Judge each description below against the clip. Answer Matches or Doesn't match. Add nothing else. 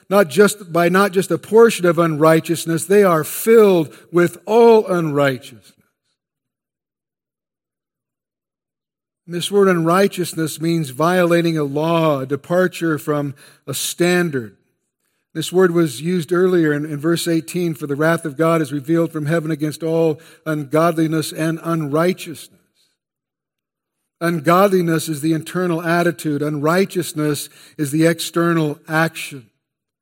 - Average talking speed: Doesn't match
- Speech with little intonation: Matches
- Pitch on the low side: Doesn't match